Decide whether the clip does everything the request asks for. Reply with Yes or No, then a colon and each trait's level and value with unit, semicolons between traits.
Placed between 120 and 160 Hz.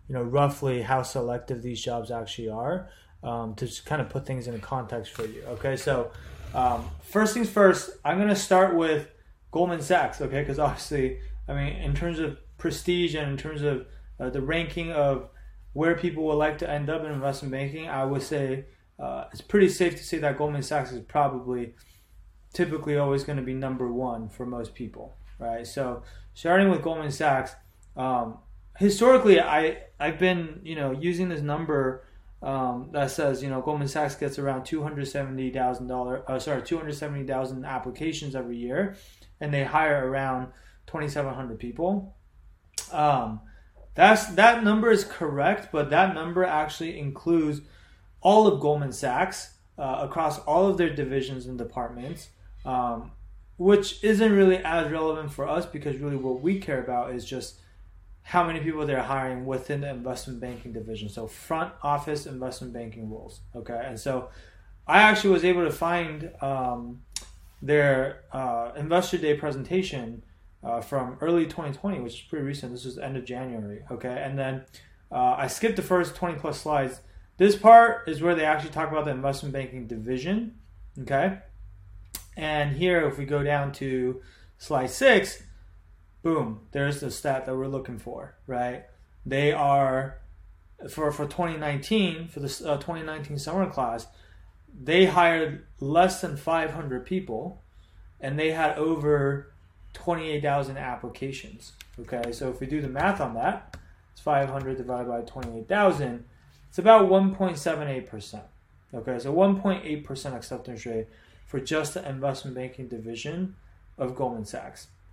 Yes: medium, 140 Hz